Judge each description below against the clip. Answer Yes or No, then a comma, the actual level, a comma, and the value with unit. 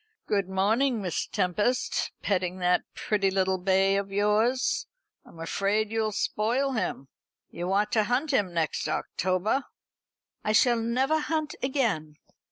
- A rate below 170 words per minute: Yes, slow, 135 wpm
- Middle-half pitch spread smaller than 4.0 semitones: No, average, 4.4 semitones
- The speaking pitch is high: Yes, high, 210 Hz